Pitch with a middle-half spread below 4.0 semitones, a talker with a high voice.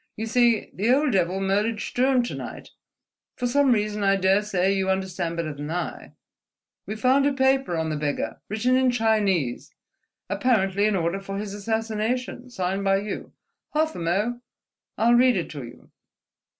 No: average, 4.3 semitones; high, 210 Hz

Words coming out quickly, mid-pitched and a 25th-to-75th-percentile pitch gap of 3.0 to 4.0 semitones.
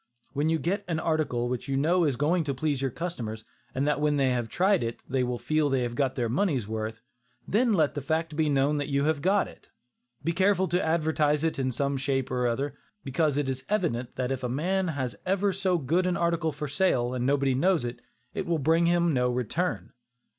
No: fast, 225 wpm; medium, 145 Hz; average, 4.6 semitones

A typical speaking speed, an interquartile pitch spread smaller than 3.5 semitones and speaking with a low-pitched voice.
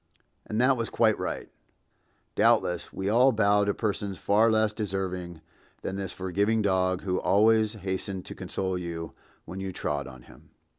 Yes: average, 160 wpm; average, 2.9 semitones; low, 100 Hz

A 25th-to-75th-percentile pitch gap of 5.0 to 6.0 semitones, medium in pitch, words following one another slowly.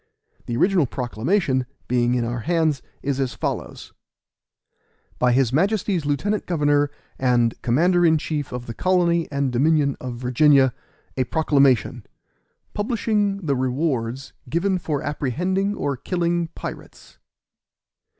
Yes: wide, 5.5 semitones; medium, 145 Hz; slow, 120 wpm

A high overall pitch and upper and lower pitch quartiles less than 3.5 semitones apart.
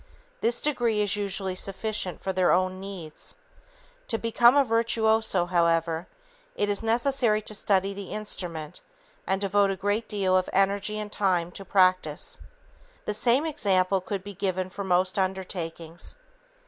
Yes: high, 195 Hz; narrow, 2.5 semitones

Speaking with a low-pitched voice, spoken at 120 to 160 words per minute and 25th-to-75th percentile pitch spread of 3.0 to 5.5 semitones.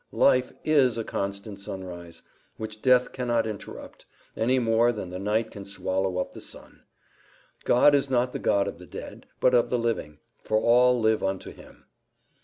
No: low, 110 Hz; average, 175 wpm; average, 4.0 semitones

